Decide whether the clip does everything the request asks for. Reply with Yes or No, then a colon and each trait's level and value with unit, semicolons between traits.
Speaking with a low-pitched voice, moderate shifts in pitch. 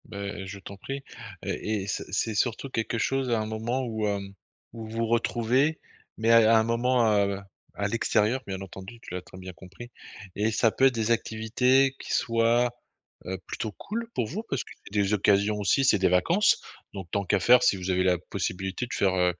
Yes: low, 110 Hz; average, 3.4 semitones